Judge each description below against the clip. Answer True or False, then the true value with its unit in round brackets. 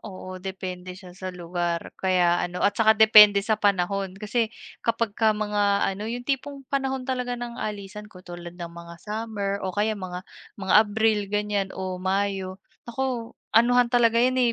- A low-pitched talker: False (205 Hz)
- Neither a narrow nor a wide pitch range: True (3.5 semitones)